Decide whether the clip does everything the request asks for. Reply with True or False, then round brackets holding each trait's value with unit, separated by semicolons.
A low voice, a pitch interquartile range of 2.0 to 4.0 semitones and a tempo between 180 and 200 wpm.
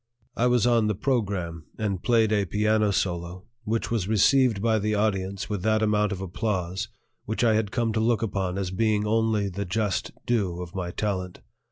True (105 Hz; 2.7 semitones; 190 wpm)